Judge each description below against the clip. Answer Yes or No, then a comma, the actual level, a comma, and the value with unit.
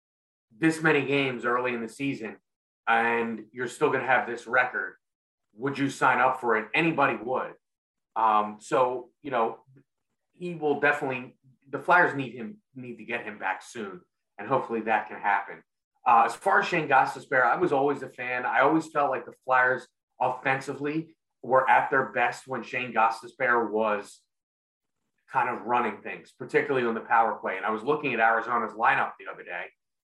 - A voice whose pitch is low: Yes, low, 125 Hz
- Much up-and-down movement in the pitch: No, average, 3.6 semitones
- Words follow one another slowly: No, average, 180 wpm